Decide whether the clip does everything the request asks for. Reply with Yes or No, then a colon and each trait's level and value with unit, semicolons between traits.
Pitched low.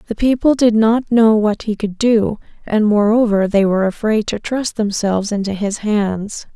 No: high, 215 Hz